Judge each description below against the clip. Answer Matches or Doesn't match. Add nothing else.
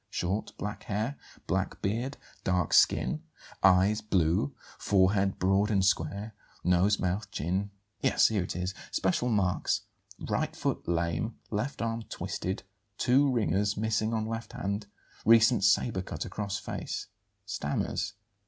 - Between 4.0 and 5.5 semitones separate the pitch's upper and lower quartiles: Doesn't match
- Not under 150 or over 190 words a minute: Doesn't match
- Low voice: Matches